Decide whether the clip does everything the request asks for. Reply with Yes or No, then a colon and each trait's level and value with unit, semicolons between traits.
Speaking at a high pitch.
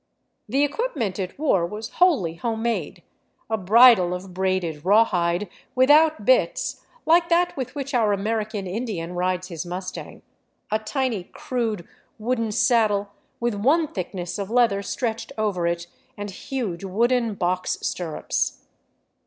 Yes: high, 215 Hz